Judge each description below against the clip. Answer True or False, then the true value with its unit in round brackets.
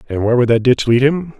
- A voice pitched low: True (130 Hz)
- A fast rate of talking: True (300 wpm)